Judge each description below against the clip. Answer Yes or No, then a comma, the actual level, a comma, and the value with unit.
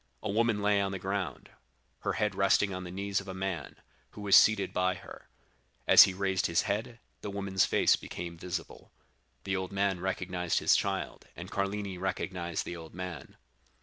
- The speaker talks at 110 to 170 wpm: No, average, 180 wpm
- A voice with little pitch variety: Yes, narrow, 1.6 semitones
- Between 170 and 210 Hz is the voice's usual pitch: No, very low, 95 Hz